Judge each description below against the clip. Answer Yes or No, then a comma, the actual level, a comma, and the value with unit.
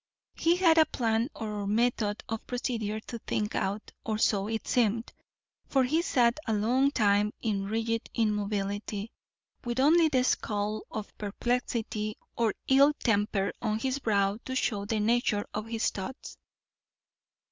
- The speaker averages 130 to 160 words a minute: Yes, average, 145 wpm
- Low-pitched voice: No, high, 225 Hz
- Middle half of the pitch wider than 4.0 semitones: No, average, 3.0 semitones